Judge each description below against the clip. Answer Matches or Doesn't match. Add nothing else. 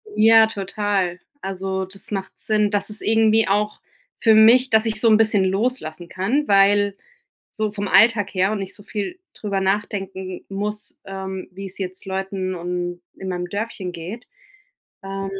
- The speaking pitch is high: Matches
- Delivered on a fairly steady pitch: Matches